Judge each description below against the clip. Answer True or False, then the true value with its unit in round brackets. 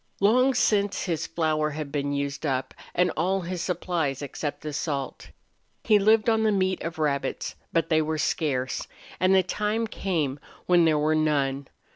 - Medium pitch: True (160 Hz)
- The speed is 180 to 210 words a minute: False (170 wpm)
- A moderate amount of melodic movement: True (4.9 semitones)